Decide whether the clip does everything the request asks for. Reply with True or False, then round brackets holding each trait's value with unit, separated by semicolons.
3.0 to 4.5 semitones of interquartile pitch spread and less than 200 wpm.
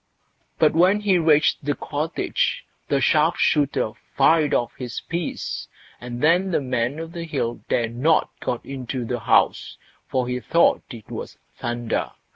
False (5.0 semitones; 155 wpm)